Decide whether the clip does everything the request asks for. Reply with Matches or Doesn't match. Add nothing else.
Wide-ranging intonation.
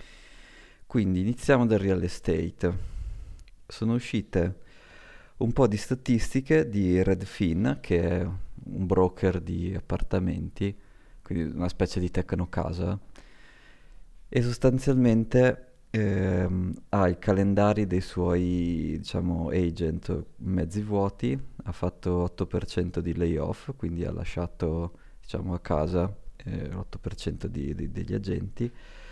Doesn't match